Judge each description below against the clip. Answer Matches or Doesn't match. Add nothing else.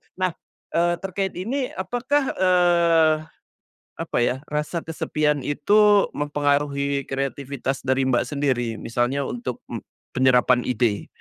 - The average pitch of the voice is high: Doesn't match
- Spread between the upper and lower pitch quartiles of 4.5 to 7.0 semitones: Matches